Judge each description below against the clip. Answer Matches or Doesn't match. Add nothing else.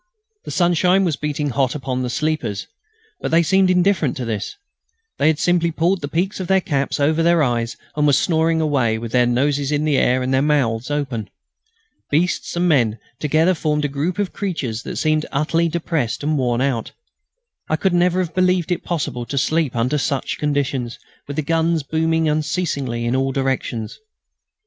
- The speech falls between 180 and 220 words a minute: Matches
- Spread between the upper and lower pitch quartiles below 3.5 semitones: Doesn't match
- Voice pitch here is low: Doesn't match